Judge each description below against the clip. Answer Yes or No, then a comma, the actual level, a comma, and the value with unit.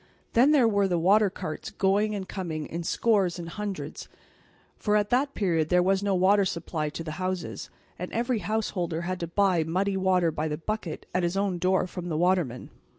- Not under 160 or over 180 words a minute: No, fast, 205 wpm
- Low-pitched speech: No, medium, 185 Hz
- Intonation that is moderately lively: Yes, average, 3.0 semitones